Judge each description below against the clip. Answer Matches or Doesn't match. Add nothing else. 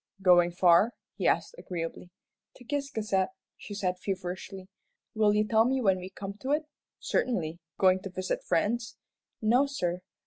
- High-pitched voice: Matches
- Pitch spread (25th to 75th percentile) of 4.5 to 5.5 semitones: Doesn't match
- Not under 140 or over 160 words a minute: Matches